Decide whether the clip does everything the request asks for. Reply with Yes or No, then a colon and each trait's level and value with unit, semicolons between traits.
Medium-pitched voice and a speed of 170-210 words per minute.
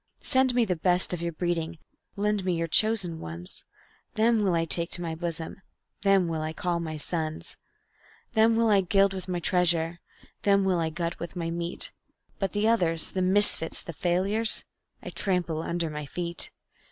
Yes: medium, 175 Hz; average, 180 wpm